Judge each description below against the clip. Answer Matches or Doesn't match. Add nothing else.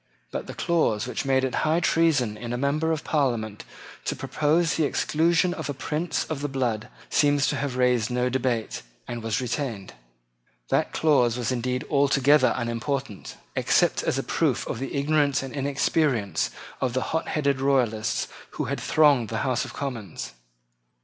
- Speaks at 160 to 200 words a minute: Matches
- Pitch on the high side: Doesn't match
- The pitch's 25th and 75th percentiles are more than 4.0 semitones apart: Doesn't match